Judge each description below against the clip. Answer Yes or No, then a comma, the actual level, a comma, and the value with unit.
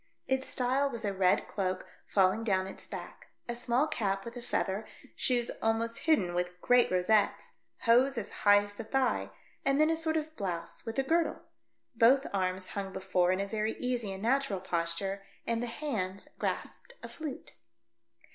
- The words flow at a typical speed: Yes, average, 175 wpm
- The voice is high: Yes, high, 225 Hz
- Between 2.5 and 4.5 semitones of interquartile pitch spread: No, average, 5.2 semitones